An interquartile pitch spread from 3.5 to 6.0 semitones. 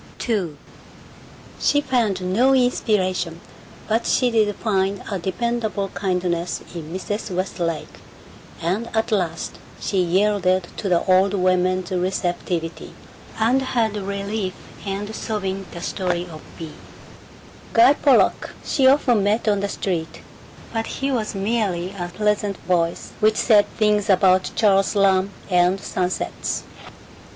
No: average, 3.0 semitones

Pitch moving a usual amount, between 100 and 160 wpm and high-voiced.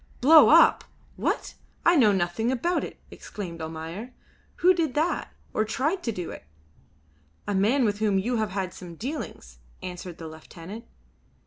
No: wide, 6.6 semitones; average, 150 wpm; high, 210 Hz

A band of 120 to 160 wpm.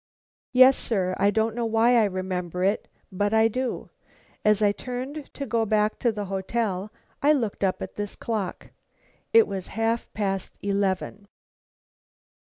Yes: average, 155 wpm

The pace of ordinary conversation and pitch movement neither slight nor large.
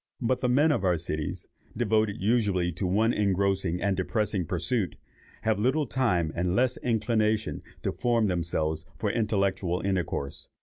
Yes: average, 145 wpm; average, 4.3 semitones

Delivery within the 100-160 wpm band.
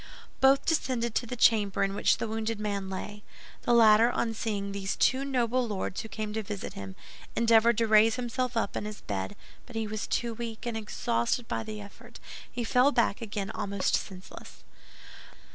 No: average, 185 wpm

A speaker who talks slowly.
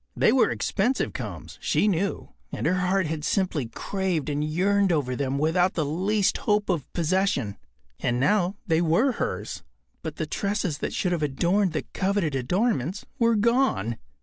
No: average, 165 wpm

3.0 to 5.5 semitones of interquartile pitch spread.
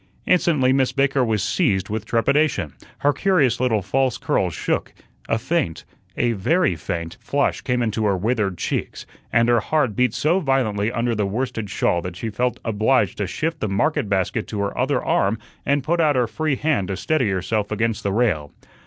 Yes: average, 5.1 semitones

